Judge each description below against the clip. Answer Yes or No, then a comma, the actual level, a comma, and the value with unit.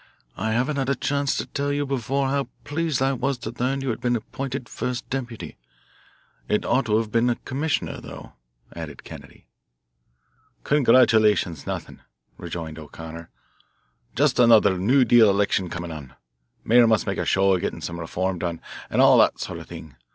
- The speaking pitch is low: Yes, low, 115 Hz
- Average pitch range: No, wide, 6.3 semitones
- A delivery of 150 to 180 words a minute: Yes, average, 170 wpm